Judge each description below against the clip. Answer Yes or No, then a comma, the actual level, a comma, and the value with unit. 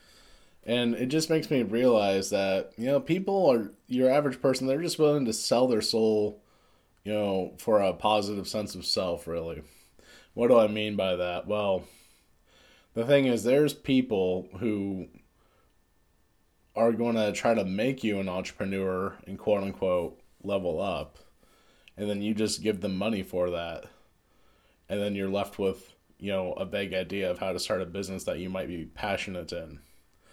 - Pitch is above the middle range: No, low, 100 Hz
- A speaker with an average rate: Yes, average, 175 wpm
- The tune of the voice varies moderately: Yes, average, 3.6 semitones